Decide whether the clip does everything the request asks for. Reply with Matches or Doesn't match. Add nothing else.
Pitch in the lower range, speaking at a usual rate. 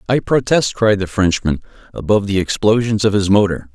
Matches